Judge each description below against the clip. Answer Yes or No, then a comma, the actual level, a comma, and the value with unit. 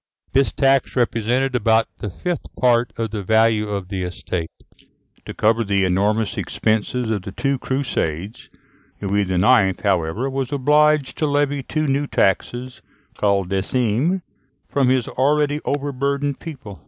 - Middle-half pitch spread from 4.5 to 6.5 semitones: Yes, average, 5.3 semitones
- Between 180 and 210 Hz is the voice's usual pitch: No, low, 120 Hz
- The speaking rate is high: No, average, 140 wpm